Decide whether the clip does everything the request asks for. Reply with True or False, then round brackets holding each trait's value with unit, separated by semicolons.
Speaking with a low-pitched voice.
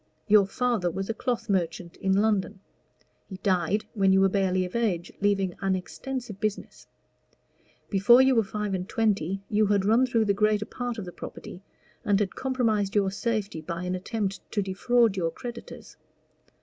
False (200 Hz)